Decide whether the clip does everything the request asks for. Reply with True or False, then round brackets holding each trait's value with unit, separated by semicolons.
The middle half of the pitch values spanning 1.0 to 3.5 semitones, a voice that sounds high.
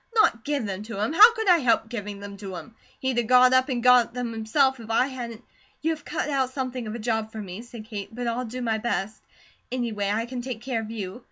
True (2.8 semitones; 235 Hz)